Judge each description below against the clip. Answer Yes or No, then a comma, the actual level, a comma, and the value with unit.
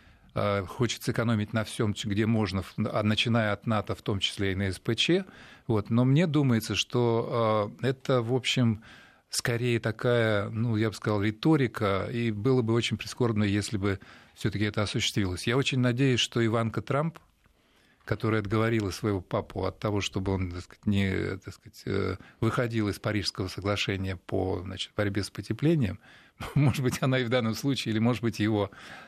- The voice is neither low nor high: No, low, 110 Hz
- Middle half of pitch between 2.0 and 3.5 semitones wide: Yes, average, 2.9 semitones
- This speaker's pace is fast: Yes, fast, 165 wpm